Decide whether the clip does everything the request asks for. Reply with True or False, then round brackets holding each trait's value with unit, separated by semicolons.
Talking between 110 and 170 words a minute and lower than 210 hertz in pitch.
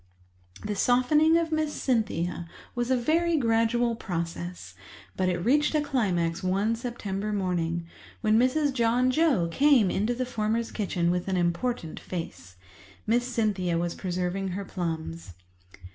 False (140 wpm; 215 Hz)